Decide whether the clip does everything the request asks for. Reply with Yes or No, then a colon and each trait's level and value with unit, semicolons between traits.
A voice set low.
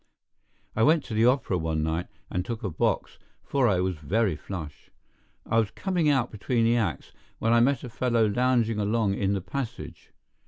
Yes: low, 110 Hz